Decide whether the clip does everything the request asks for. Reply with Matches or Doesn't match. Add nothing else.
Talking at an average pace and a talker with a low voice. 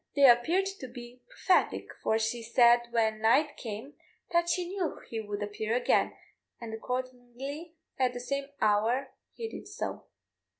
Doesn't match